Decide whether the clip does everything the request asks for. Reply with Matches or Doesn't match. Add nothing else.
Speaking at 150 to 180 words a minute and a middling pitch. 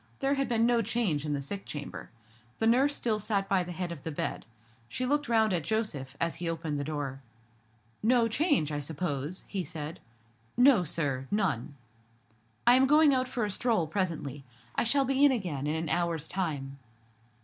Doesn't match